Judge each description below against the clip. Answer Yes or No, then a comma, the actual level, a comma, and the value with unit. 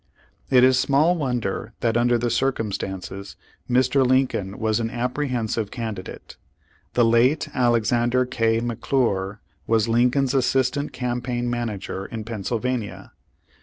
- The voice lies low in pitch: Yes, low, 120 Hz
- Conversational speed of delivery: No, slow, 115 wpm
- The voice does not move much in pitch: Yes, narrow, 2.2 semitones